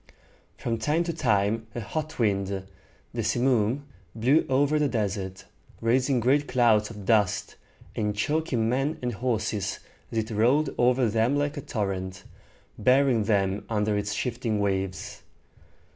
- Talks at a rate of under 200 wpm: Yes, average, 140 wpm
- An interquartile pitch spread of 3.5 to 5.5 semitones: Yes, average, 4.2 semitones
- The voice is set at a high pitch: No, low, 115 Hz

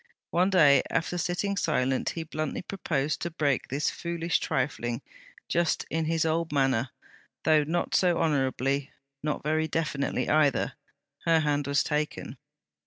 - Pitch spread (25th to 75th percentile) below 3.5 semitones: Yes, average, 2.9 semitones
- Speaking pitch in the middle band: Yes, medium, 155 Hz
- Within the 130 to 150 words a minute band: Yes, average, 140 wpm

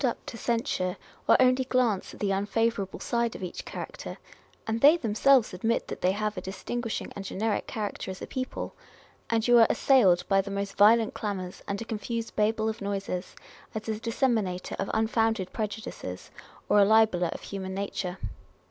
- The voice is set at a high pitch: Yes, high, 215 Hz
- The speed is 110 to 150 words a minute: No, average, 175 wpm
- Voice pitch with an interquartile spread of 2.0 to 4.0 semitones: Yes, average, 2.8 semitones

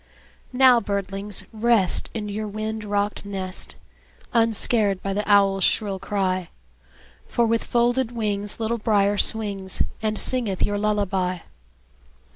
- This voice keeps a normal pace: No, slow, 120 wpm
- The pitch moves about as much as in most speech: No, narrow, 2.1 semitones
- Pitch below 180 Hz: No, high, 205 Hz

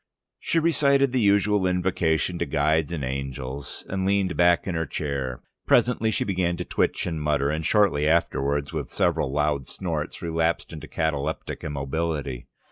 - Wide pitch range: No, average, 4.5 semitones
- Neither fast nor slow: Yes, average, 155 wpm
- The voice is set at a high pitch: No, very low, 80 Hz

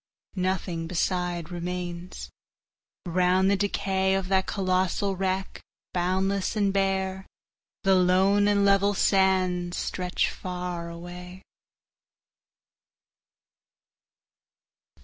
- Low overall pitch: No, medium, 185 Hz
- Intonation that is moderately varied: No, narrow, 1.3 semitones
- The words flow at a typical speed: No, slow, 75 wpm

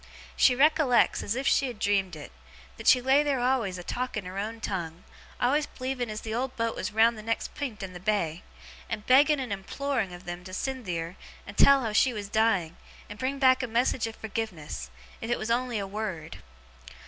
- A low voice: No, high, 225 Hz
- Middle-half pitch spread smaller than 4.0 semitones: No, average, 4.9 semitones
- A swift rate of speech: Yes, fast, 210 wpm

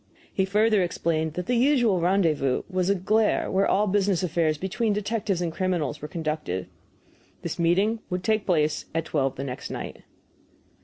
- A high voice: No, medium, 180 Hz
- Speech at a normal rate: Yes, average, 165 wpm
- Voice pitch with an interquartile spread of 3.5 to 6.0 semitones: Yes, average, 4.3 semitones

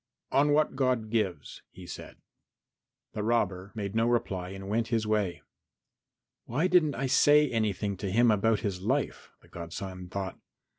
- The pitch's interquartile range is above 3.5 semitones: Yes, average, 4.1 semitones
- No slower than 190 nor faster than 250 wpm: No, average, 155 wpm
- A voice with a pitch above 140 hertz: No, low, 110 Hz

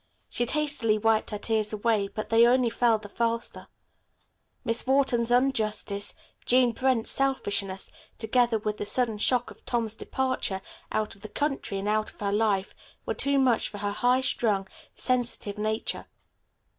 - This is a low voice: No, high, 225 Hz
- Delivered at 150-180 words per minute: Yes, average, 155 wpm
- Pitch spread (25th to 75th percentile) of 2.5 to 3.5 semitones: Yes, average, 2.9 semitones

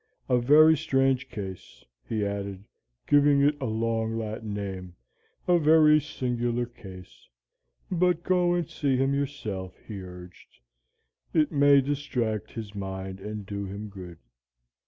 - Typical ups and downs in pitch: No, wide, 6.2 semitones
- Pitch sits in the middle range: No, low, 115 Hz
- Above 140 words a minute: No, slow, 135 wpm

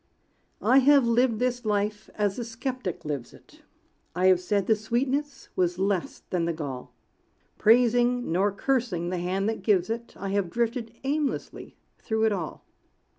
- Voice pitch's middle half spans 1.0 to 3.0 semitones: No, average, 4.8 semitones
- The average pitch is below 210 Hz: No, high, 215 Hz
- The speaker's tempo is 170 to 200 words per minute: No, average, 160 wpm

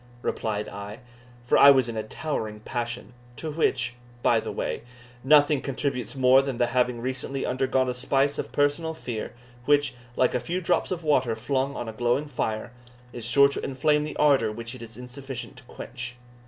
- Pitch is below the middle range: Yes, low, 130 Hz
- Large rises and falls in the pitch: No, average, 2.9 semitones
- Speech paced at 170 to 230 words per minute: Yes, average, 185 wpm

